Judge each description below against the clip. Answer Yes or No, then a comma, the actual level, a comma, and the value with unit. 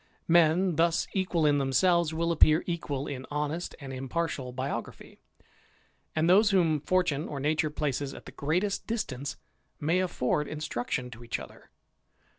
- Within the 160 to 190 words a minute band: No, average, 140 wpm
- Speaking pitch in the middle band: Yes, medium, 155 Hz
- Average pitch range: Yes, average, 3.6 semitones